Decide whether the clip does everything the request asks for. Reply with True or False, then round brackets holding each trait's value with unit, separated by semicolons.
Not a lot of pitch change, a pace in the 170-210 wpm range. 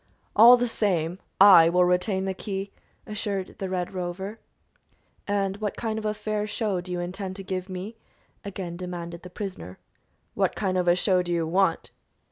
True (2.3 semitones; 180 wpm)